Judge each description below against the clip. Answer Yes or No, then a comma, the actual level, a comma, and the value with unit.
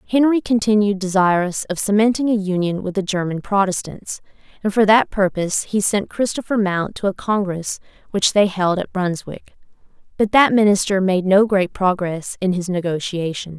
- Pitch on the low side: No, high, 195 Hz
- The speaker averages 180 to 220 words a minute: No, average, 165 wpm